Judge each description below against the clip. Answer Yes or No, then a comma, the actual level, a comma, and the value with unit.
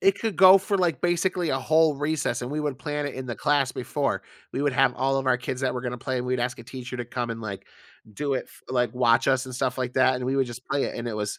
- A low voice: Yes, low, 130 Hz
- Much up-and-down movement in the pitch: No, average, 3.0 semitones